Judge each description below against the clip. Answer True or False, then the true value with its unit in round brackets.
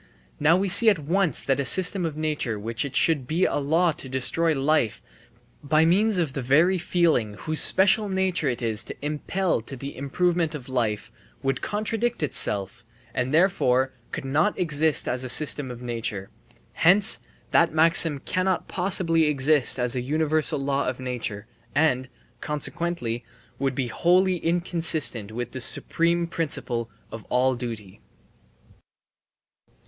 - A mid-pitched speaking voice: True (150 Hz)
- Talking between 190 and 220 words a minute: False (155 wpm)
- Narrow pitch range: False (5.3 semitones)